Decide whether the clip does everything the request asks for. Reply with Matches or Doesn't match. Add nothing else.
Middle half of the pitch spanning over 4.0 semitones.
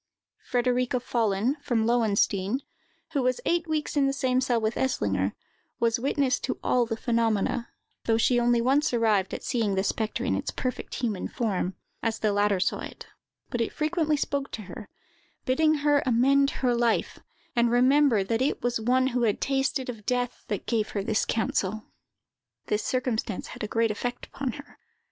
Doesn't match